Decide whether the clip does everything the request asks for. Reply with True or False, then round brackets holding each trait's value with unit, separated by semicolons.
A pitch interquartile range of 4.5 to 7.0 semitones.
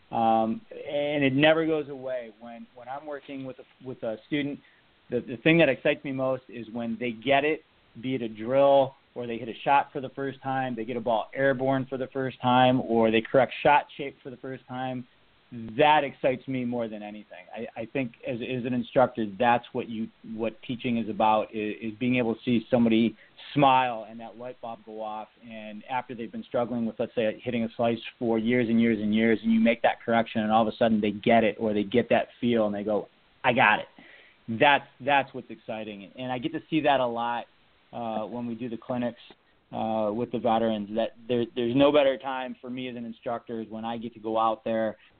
False (2.5 semitones)